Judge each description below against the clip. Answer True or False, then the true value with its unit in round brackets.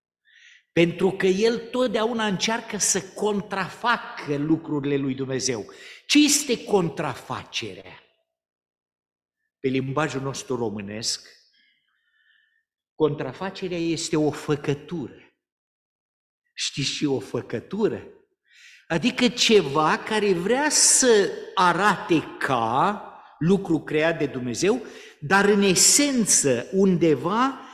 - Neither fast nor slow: False (85 wpm)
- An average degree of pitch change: False (8.8 semitones)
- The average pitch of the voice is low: False (190 Hz)